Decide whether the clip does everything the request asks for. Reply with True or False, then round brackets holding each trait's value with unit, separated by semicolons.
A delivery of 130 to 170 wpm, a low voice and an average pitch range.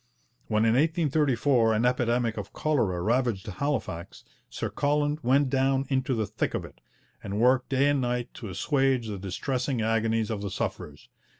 True (165 wpm; 125 Hz; 3.6 semitones)